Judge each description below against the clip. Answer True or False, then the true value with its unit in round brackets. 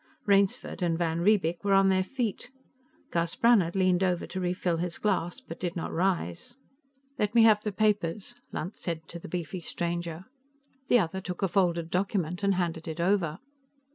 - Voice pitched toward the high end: False (180 Hz)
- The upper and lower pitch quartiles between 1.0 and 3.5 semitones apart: True (2.7 semitones)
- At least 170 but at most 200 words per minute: True (175 wpm)